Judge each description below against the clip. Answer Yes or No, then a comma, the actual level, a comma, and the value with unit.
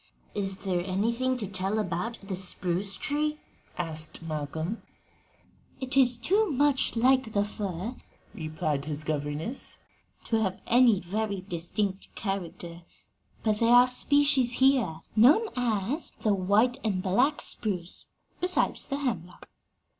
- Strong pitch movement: Yes, wide, 5.7 semitones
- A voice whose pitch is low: No, high, 205 Hz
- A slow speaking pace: Yes, slow, 125 wpm